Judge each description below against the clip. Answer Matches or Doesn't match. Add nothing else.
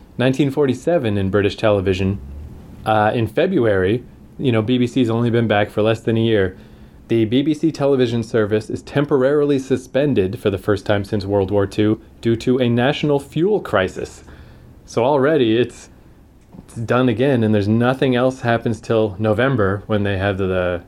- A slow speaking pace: Doesn't match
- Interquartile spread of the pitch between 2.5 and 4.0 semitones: Matches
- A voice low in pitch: Matches